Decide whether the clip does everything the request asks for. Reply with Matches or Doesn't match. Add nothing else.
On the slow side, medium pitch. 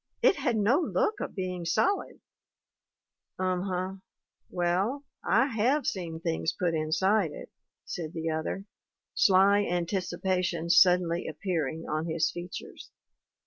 Matches